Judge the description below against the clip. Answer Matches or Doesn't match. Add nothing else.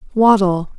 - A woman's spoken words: Matches